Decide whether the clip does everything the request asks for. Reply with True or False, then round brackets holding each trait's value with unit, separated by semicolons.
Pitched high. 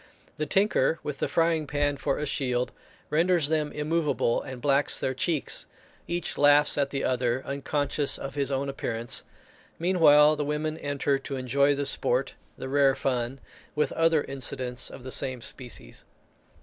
False (140 Hz)